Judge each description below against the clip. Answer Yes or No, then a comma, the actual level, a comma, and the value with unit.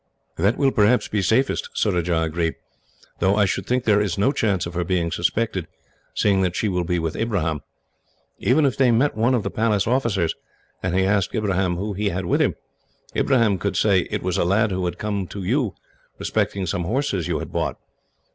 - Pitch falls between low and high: No, low, 100 Hz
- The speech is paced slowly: No, fast, 205 wpm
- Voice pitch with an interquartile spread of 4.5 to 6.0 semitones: No, average, 3.9 semitones